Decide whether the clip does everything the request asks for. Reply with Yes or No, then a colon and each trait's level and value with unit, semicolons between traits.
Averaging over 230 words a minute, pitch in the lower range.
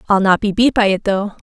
No: fast, 285 wpm; high, 200 Hz